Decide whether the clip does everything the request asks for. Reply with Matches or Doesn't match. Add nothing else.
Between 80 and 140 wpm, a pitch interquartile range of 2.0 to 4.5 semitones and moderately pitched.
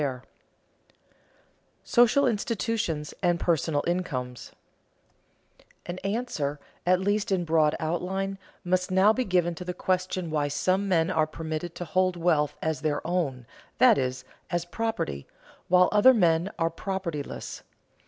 Matches